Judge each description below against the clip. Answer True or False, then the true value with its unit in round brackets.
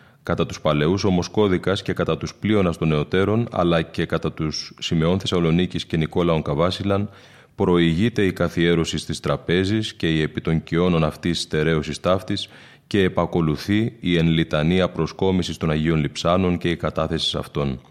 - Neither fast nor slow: True (145 wpm)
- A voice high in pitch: False (85 Hz)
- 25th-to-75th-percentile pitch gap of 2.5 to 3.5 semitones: True (2.8 semitones)